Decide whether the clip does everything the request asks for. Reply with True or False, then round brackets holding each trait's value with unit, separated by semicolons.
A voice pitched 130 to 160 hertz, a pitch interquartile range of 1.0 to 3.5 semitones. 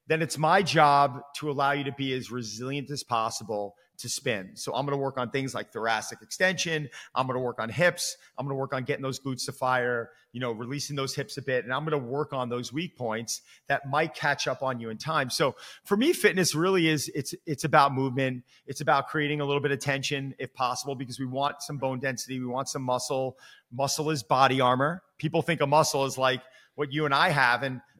True (140 Hz; 2.9 semitones)